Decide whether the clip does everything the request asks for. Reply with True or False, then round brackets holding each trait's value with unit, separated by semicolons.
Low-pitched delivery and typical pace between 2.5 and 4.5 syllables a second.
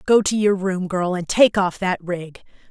False (185 Hz; 4.4 syllables/s)